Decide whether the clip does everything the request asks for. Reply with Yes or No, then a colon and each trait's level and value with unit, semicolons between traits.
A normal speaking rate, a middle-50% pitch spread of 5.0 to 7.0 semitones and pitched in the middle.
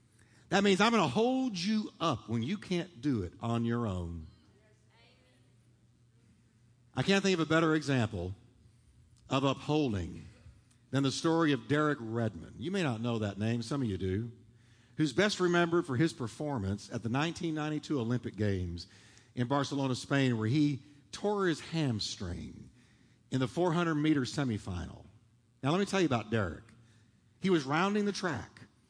No: average, 160 wpm; wide, 5.6 semitones; low, 125 Hz